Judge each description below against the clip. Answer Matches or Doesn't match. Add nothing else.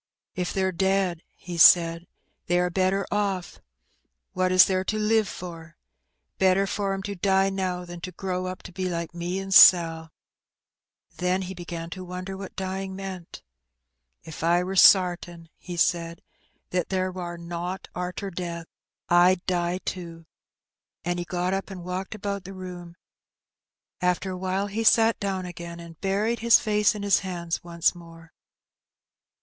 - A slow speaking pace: Doesn't match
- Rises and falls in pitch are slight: Matches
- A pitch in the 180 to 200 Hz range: Matches